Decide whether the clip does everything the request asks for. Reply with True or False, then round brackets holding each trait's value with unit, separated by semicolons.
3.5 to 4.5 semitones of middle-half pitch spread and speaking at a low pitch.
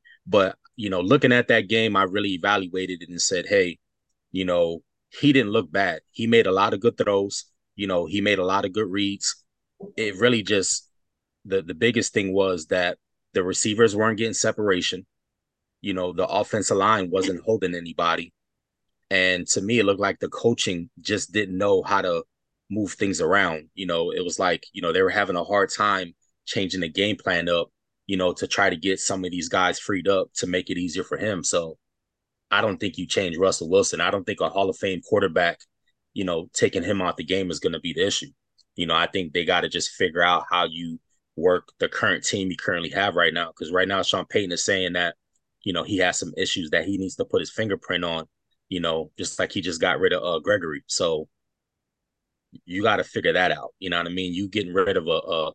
True (3.9 semitones; 95 Hz)